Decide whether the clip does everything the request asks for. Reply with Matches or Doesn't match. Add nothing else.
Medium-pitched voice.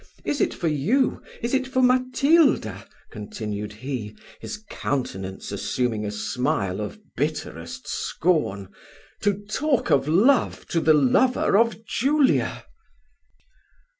Matches